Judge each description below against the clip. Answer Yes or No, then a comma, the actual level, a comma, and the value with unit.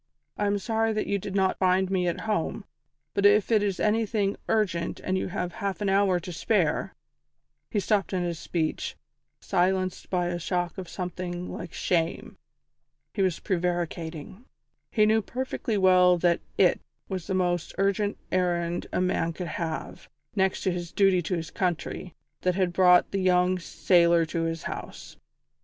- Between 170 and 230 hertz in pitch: Yes, medium, 185 Hz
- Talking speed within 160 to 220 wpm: Yes, average, 170 wpm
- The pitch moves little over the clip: Yes, narrow, 2.2 semitones